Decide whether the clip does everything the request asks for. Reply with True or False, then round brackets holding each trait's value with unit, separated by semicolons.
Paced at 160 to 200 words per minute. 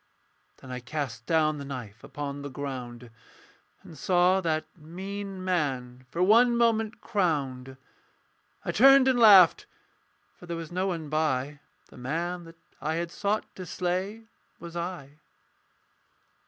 False (140 wpm)